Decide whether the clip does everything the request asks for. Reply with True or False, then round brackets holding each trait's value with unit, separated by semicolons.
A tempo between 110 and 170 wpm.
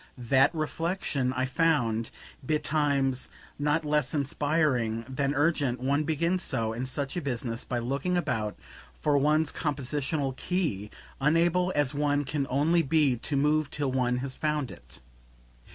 True (140 wpm)